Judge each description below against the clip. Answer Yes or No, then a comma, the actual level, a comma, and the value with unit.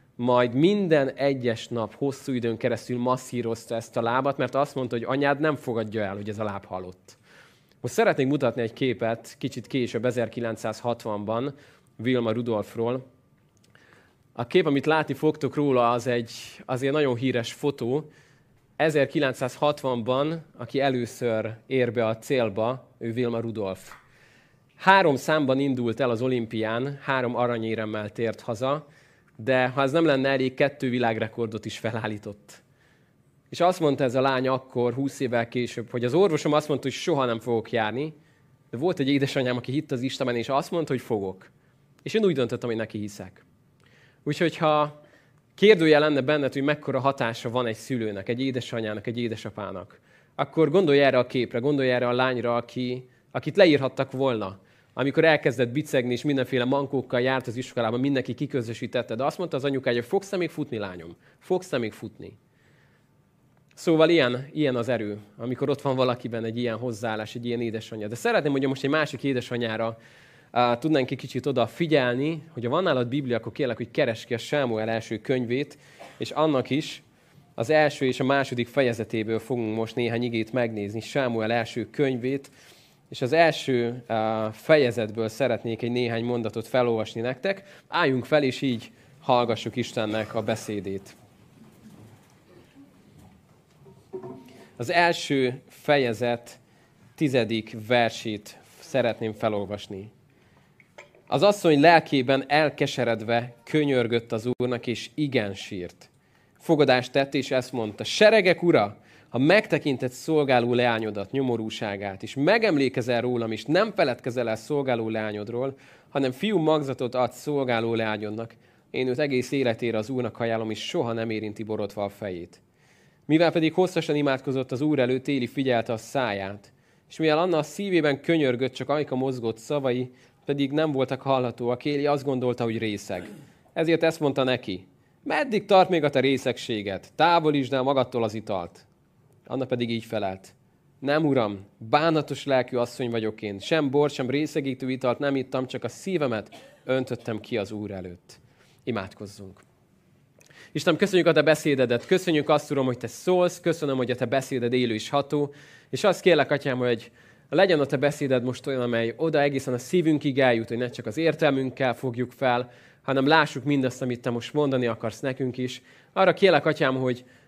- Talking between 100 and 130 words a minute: No, fast, 155 wpm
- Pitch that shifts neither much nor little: Yes, average, 3.7 semitones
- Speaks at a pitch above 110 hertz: Yes, low, 125 Hz